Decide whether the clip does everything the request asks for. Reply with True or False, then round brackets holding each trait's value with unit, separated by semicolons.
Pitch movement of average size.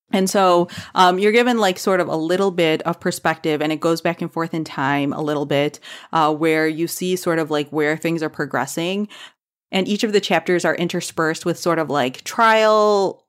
True (3.2 semitones)